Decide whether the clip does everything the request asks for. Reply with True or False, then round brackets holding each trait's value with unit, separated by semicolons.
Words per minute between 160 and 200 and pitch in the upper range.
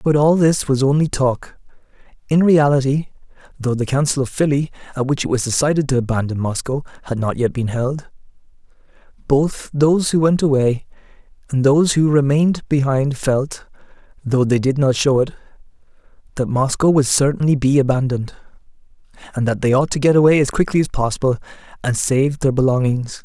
False (165 wpm; 135 Hz)